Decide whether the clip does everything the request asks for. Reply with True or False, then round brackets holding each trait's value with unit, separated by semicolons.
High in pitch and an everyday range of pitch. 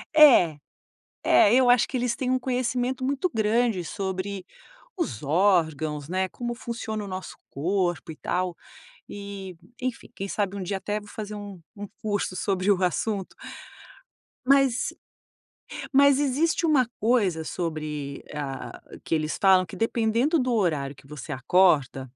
False (200 Hz; 5.7 semitones)